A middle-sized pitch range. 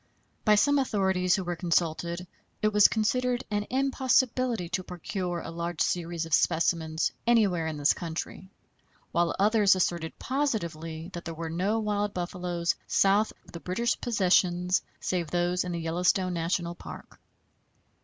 Yes: average, 3.6 semitones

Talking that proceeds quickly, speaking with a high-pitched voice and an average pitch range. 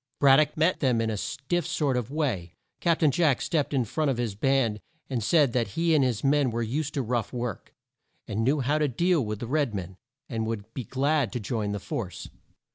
No: fast, 225 wpm; low, 130 Hz; average, 4.8 semitones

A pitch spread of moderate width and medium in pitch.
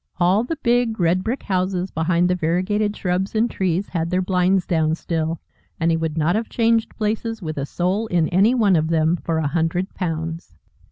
Yes: average, 4.0 semitones; medium, 180 Hz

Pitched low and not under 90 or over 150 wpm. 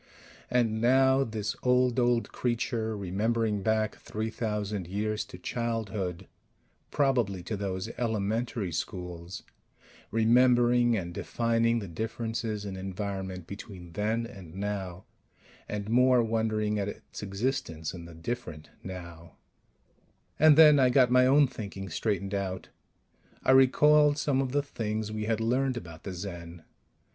Yes: low, 110 Hz; slow, 135 wpm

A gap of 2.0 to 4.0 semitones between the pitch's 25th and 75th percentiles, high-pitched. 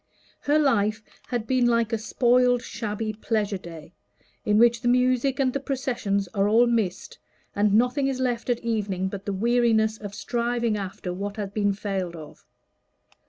Yes: average, 3.3 semitones; high, 225 Hz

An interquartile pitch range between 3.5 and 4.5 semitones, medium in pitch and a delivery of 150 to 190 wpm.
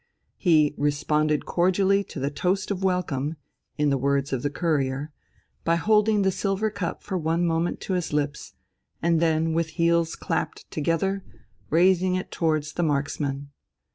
Yes: average, 3.8 semitones; medium, 165 Hz; average, 155 wpm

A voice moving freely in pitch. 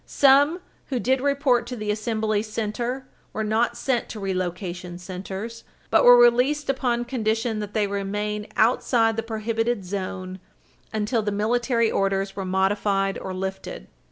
No: average, 3.5 semitones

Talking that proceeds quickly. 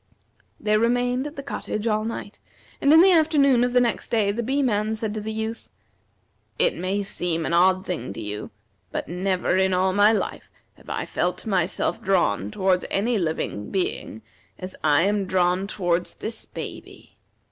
No: average, 180 wpm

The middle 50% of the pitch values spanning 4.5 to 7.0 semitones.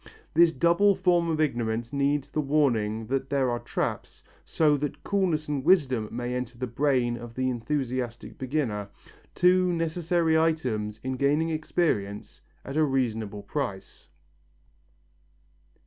Yes: average, 4.9 semitones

